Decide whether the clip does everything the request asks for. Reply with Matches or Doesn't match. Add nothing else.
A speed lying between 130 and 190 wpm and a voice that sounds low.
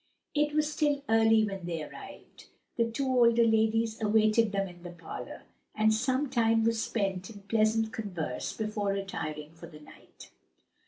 Doesn't match